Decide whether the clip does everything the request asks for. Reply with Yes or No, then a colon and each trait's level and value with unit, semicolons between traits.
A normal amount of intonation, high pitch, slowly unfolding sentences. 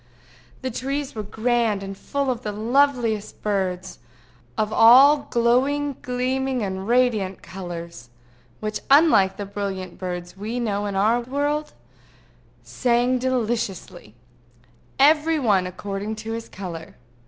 Yes: average, 4.7 semitones; high, 225 Hz; slow, 120 wpm